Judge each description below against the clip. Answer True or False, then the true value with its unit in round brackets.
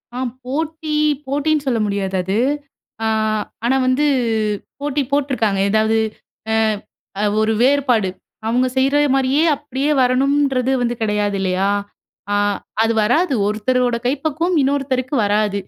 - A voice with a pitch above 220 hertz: True (255 Hz)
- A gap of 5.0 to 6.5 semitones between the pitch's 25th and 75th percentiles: False (4.6 semitones)